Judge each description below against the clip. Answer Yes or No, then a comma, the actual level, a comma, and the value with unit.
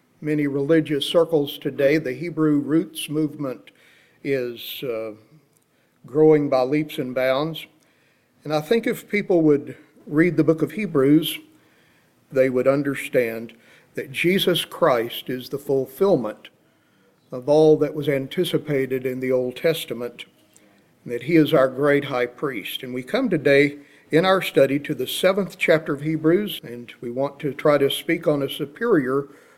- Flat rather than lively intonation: No, average, 3.1 semitones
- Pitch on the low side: No, medium, 150 Hz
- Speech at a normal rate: Yes, average, 150 wpm